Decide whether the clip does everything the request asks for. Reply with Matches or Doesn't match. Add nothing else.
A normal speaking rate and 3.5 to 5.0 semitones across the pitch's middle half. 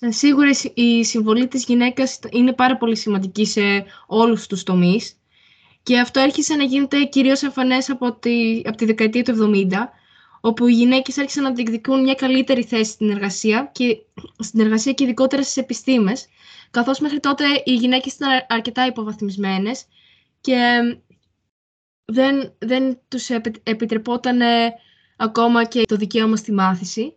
Doesn't match